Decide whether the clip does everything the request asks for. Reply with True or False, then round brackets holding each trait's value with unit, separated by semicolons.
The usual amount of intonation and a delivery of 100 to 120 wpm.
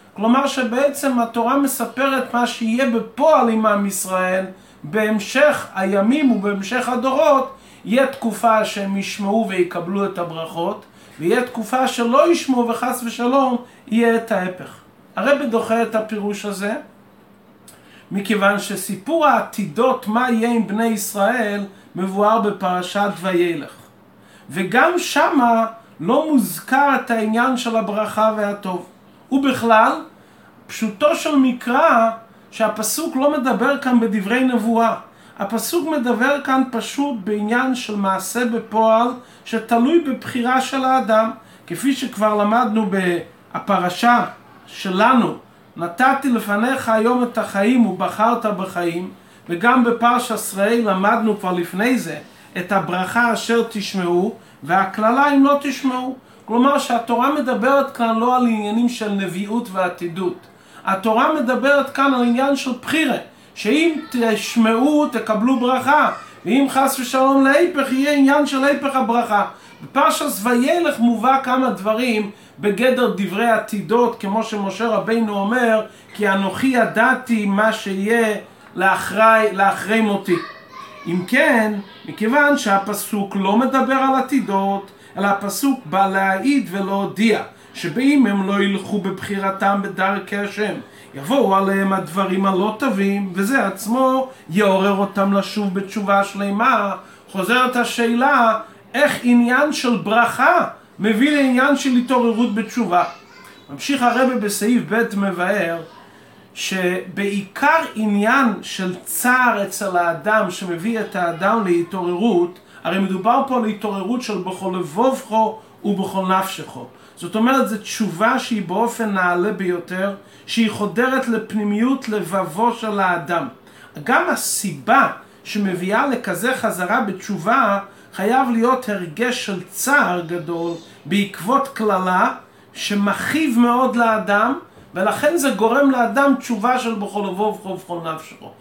True (4.3 semitones; 115 wpm)